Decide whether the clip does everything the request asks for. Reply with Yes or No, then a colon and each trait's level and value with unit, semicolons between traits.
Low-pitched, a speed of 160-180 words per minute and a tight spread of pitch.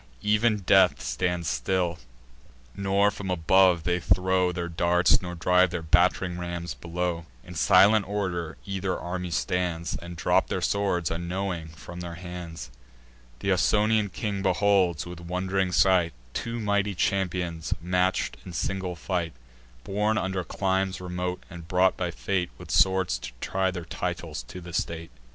No: very low, 90 Hz; average, 145 wpm; narrow, 1.9 semitones